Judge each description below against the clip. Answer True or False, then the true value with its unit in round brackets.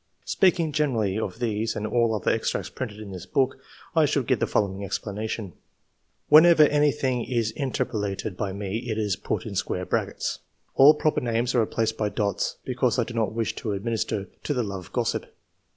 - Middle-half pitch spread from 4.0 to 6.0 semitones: False (3.6 semitones)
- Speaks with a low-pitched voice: True (110 Hz)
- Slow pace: False (200 wpm)